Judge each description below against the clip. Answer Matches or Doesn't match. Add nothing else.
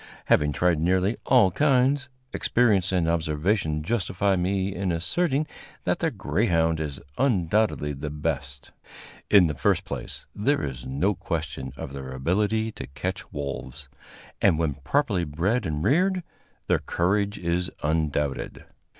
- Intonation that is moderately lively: Doesn't match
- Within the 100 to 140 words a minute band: Matches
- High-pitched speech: Doesn't match